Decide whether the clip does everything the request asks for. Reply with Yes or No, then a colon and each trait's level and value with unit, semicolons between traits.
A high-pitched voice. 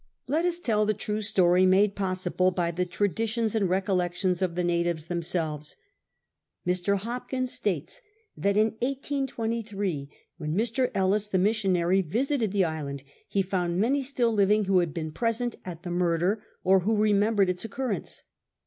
Yes: high, 195 Hz